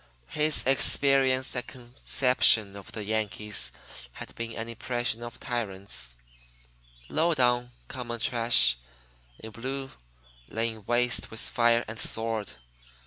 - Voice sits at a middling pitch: No, low, 120 Hz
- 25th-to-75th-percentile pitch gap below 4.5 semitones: Yes, narrow, 2.4 semitones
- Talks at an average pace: No, slow, 115 wpm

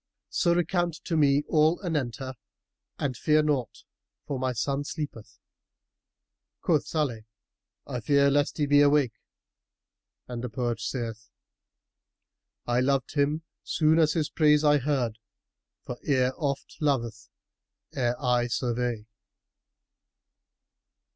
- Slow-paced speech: Yes, slow, 120 wpm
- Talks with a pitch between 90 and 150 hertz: Yes, medium, 140 Hz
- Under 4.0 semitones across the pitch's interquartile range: Yes, average, 3.6 semitones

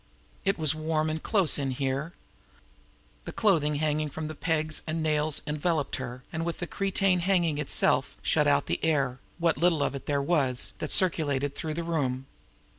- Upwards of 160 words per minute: Yes, average, 175 wpm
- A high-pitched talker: No, medium, 155 Hz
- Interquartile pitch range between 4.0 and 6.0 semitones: No, average, 2.7 semitones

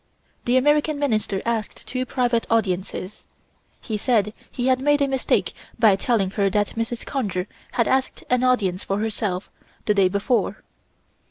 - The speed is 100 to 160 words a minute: Yes, average, 155 wpm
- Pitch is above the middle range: Yes, high, 230 Hz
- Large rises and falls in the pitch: No, average, 4.1 semitones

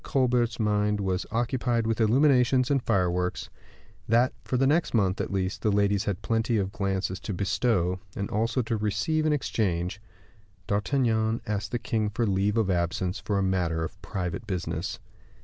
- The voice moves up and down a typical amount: Yes, average, 3.8 semitones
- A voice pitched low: Yes, low, 105 Hz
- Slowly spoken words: No, average, 165 wpm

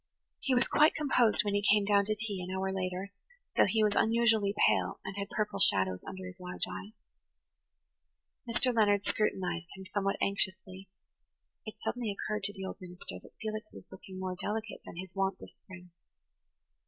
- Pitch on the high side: Yes, high, 200 Hz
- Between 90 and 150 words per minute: No, average, 180 wpm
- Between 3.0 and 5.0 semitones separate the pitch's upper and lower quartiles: No, narrow, 2.4 semitones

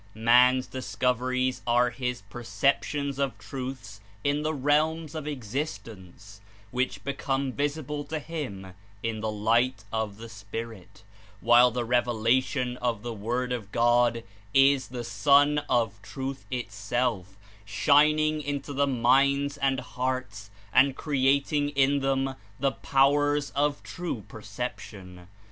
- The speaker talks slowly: Yes, slow, 125 wpm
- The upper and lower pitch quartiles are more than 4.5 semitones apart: No, average, 3.8 semitones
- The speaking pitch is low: Yes, low, 125 Hz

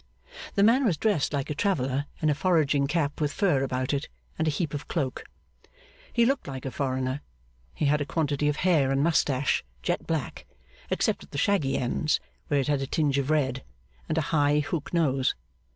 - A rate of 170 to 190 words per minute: No, average, 200 wpm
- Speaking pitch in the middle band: Yes, medium, 145 Hz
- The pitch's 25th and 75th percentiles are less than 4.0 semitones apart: Yes, average, 2.9 semitones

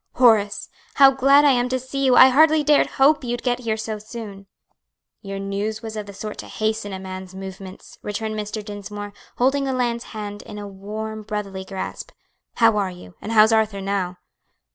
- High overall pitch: Yes, high, 215 Hz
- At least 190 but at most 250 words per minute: Yes, average, 195 wpm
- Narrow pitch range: No, average, 3.5 semitones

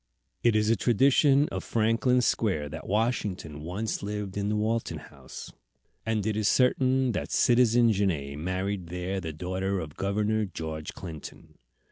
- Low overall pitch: Yes, low, 105 Hz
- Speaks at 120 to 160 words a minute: Yes, average, 150 wpm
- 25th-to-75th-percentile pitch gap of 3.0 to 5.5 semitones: Yes, average, 4.2 semitones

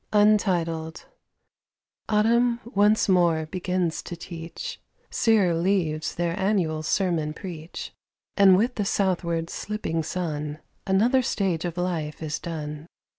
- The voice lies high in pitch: No, medium, 175 Hz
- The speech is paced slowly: Yes, slow, 110 wpm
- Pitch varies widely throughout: No, average, 3.6 semitones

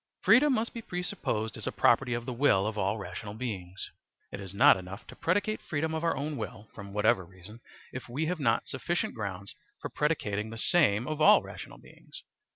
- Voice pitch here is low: Yes, low, 115 Hz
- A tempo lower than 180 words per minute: No, average, 200 wpm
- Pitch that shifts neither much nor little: No, wide, 7.8 semitones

